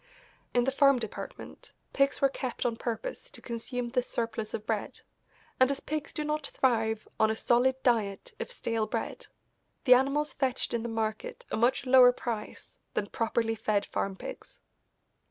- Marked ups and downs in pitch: No, average, 3.2 semitones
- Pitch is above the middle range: Yes, high, 240 Hz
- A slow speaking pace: No, average, 170 wpm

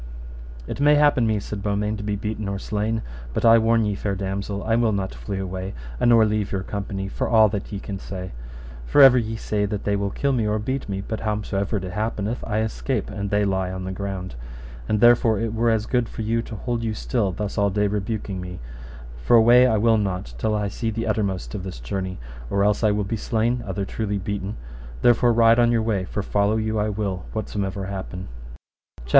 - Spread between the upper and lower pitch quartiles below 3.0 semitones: Yes, narrow, 2.4 semitones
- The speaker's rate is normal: No, fast, 225 wpm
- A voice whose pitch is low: Yes, low, 105 Hz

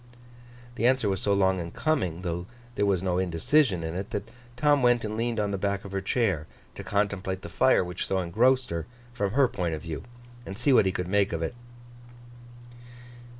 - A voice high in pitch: No, low, 100 Hz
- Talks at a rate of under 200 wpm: No, fast, 205 wpm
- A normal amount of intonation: Yes, average, 4.7 semitones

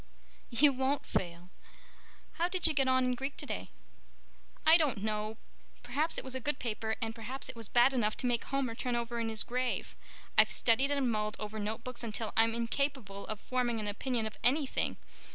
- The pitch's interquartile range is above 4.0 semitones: No, average, 3.3 semitones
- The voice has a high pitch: Yes, high, 240 Hz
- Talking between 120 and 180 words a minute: No, average, 190 wpm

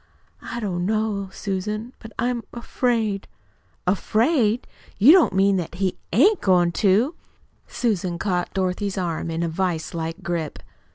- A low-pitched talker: No, high, 195 Hz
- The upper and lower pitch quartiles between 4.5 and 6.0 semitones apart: No, average, 4.0 semitones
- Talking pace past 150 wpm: No, slow, 135 wpm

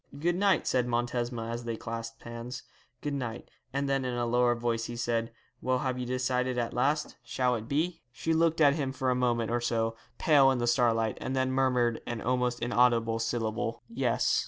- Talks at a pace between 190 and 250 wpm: Yes, average, 200 wpm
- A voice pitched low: Yes, low, 125 Hz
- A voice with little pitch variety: Yes, narrow, 1.9 semitones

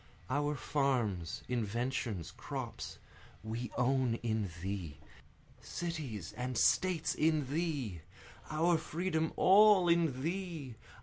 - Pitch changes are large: Yes, wide, 6.2 semitones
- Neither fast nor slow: No, slow, 100 wpm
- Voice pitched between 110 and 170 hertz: Yes, low, 135 Hz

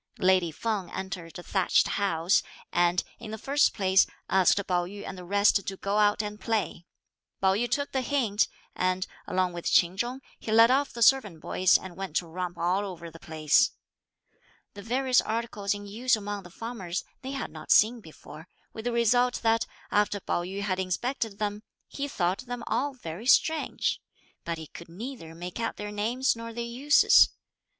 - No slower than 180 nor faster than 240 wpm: Yes, average, 185 wpm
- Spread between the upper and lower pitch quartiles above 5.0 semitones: No, average, 4.5 semitones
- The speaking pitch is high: Yes, high, 205 Hz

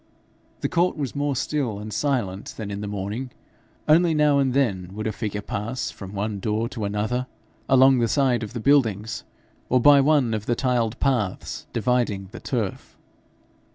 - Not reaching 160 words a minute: No, average, 175 wpm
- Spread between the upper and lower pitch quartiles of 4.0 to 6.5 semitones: Yes, average, 4.6 semitones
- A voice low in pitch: Yes, low, 120 Hz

